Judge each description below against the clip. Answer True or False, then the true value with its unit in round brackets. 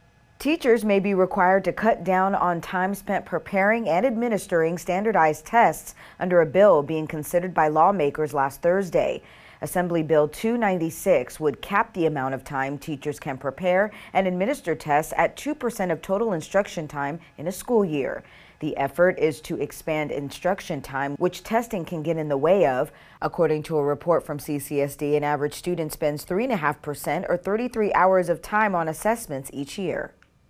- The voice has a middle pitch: True (170 Hz)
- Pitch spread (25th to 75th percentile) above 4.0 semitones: True (4.4 semitones)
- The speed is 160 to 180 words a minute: True (165 wpm)